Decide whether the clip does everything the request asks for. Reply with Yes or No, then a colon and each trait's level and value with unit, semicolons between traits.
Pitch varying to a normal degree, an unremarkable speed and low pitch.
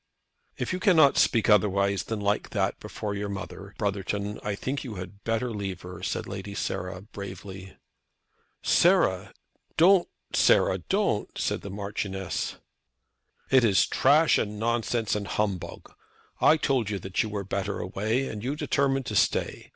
Yes: average, 3.1 semitones; average, 150 wpm; low, 105 Hz